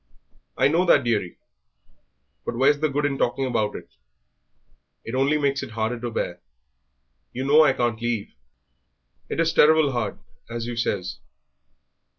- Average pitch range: Yes, average, 3.9 semitones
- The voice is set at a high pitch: No, low, 125 Hz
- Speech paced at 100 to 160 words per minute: Yes, average, 155 wpm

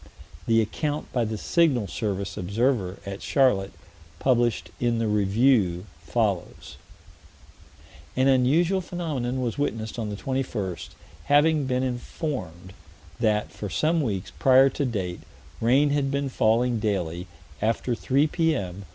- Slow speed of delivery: Yes, slow, 125 wpm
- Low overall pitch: Yes, low, 120 Hz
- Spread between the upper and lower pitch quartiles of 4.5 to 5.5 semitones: Yes, average, 5.1 semitones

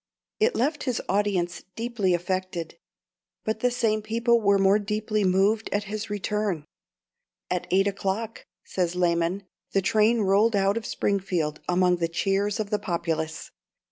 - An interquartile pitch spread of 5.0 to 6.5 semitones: No, average, 3.0 semitones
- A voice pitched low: No, high, 200 Hz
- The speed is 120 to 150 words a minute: Yes, average, 145 wpm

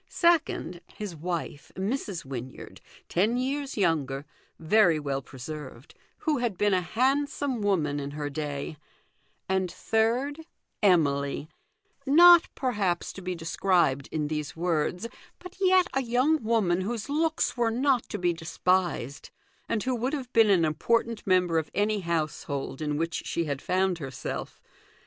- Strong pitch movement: Yes, wide, 7.6 semitones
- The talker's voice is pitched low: No, medium, 185 Hz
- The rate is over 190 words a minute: No, average, 145 wpm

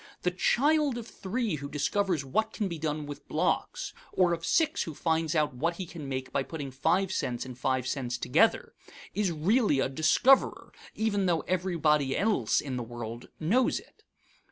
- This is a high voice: No, medium, 160 Hz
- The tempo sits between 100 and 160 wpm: No, average, 180 wpm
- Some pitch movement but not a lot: No, wide, 6.6 semitones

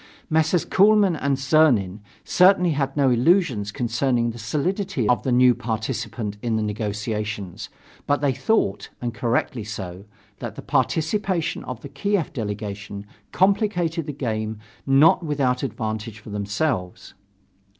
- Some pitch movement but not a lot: No, wide, 6.7 semitones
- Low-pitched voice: Yes, low, 125 Hz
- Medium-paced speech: No, slow, 130 wpm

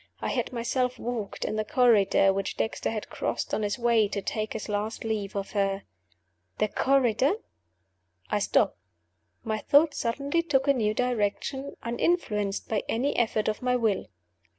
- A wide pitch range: No, average, 3.3 semitones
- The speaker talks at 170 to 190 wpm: No, average, 160 wpm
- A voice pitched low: No, high, 225 Hz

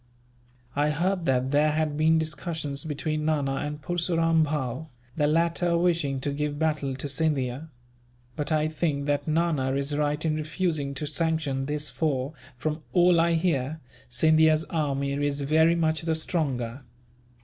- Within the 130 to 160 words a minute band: Yes, average, 150 wpm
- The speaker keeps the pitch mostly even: Yes, narrow, 2.3 semitones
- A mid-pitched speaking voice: Yes, medium, 150 Hz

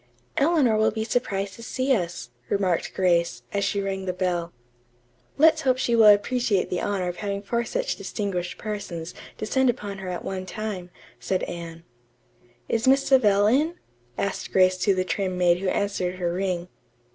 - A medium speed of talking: Yes, average, 170 wpm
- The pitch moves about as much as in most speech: Yes, average, 3.6 semitones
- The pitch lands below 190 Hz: No, high, 200 Hz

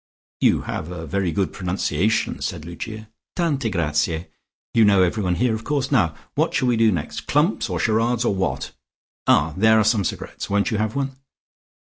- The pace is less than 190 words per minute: Yes, average, 180 wpm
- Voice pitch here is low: Yes, low, 105 Hz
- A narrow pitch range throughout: No, average, 4.6 semitones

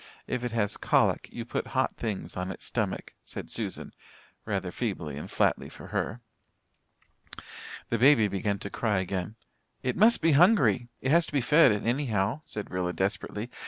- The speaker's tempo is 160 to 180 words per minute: Yes, average, 165 wpm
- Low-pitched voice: Yes, low, 110 Hz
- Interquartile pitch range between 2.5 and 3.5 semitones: No, average, 5.2 semitones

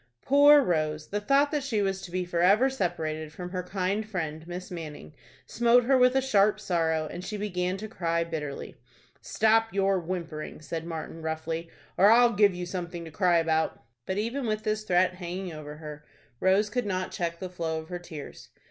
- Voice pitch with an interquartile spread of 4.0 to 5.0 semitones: Yes, average, 4.3 semitones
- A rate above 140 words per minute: Yes, average, 190 wpm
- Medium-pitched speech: Yes, medium, 180 Hz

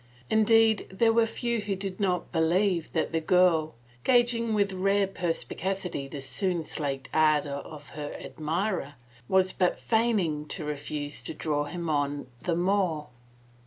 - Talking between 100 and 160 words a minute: Yes, average, 145 wpm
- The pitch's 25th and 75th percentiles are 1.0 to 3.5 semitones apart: No, average, 4.9 semitones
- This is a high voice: No, medium, 180 Hz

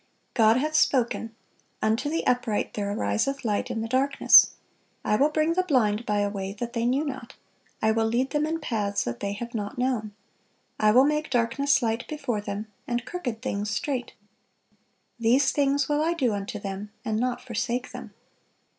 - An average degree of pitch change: Yes, average, 4.4 semitones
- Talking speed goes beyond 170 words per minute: Yes, average, 180 wpm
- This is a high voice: Yes, high, 240 Hz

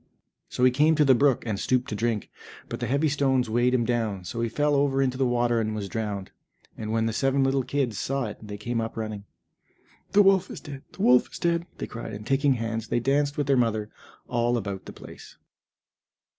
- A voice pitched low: Yes, low, 120 Hz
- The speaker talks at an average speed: No, fast, 225 wpm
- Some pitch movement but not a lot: Yes, average, 3.6 semitones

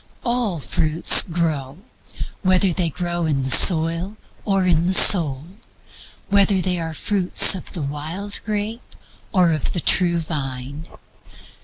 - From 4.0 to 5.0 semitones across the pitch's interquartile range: No, average, 3.6 semitones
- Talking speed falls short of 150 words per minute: Yes, average, 140 wpm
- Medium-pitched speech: Yes, medium, 175 Hz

